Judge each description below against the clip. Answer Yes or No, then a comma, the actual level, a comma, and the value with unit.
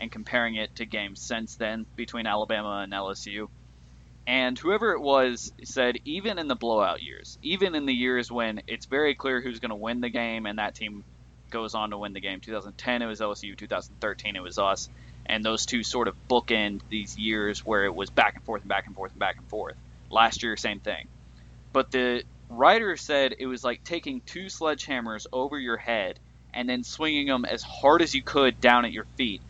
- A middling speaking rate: No, fast, 210 wpm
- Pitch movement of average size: Yes, average, 3.3 semitones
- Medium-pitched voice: No, low, 115 Hz